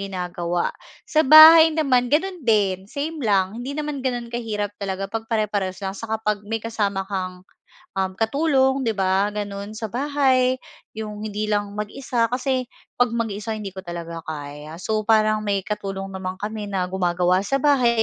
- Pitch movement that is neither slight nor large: Yes, average, 4.2 semitones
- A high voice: Yes, high, 210 Hz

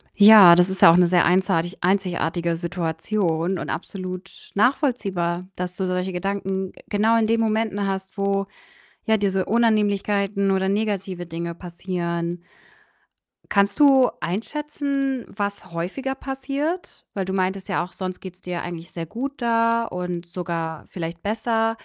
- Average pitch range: Yes, average, 3.7 semitones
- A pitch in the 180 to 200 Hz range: Yes, high, 190 Hz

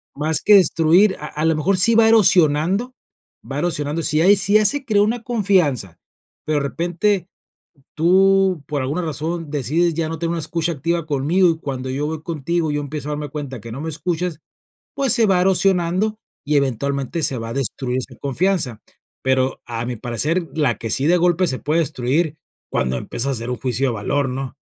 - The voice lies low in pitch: No, medium, 155 Hz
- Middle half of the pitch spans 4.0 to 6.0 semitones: Yes, average, 4.7 semitones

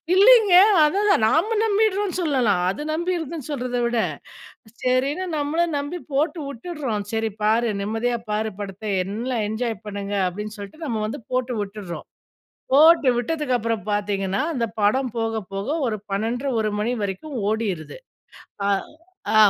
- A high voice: Yes, high, 240 Hz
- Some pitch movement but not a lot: No, wide, 6.2 semitones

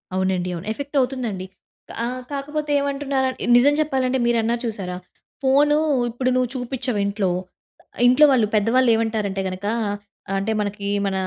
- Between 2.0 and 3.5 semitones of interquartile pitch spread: No, average, 4.9 semitones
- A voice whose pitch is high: Yes, high, 240 Hz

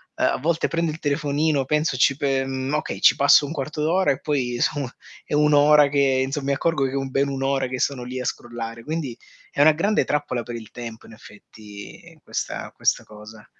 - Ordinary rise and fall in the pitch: Yes, average, 3.2 semitones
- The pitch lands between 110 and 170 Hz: Yes, medium, 140 Hz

